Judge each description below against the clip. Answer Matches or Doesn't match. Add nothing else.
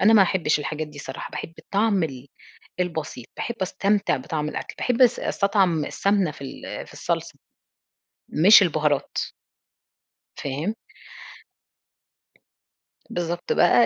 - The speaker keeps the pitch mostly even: Doesn't match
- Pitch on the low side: Doesn't match